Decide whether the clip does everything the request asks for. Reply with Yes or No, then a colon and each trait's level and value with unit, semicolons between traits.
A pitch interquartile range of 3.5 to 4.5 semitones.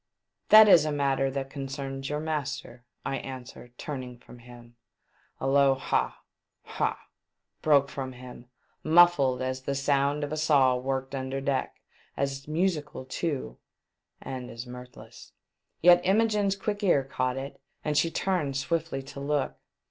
No: average, 2.7 semitones